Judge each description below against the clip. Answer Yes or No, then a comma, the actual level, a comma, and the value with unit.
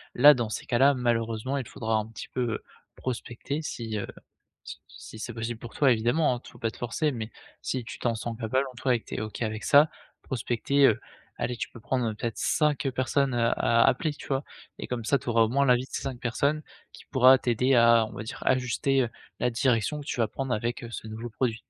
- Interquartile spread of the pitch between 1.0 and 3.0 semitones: Yes, average, 2.7 semitones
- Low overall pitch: Yes, low, 120 Hz